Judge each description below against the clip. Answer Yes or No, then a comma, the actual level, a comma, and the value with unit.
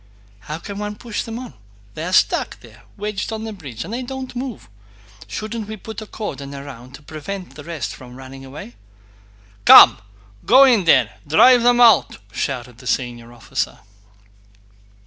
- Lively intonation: Yes, wide, 8.9 semitones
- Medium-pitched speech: Yes, medium, 180 Hz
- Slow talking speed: No, average, 165 wpm